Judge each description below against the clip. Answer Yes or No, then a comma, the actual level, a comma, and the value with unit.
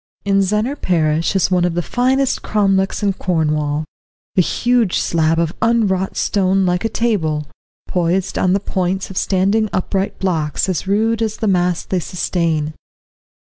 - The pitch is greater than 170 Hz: Yes, high, 190 Hz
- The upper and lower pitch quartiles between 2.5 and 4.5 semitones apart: Yes, average, 3.3 semitones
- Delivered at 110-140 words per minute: No, average, 155 wpm